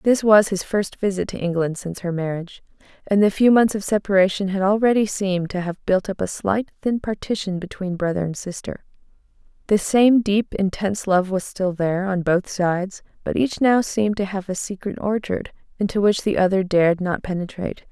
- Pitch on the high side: Yes, high, 195 Hz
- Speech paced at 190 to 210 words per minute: Yes, average, 195 wpm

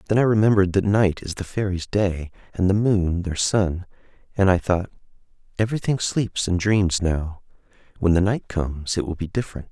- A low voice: Yes, very low, 95 Hz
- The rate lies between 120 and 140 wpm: No, average, 180 wpm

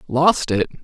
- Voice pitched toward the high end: No, medium, 145 Hz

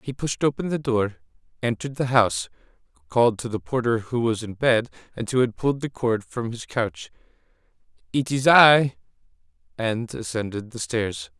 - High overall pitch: No, low, 120 Hz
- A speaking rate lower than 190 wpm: Yes, average, 170 wpm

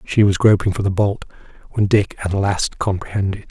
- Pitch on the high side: No, low, 100 Hz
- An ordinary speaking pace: Yes, average, 190 wpm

